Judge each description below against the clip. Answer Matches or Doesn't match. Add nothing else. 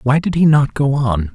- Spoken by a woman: Doesn't match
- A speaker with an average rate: Doesn't match